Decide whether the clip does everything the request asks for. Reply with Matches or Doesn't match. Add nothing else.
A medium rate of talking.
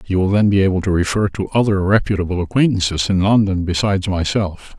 Matches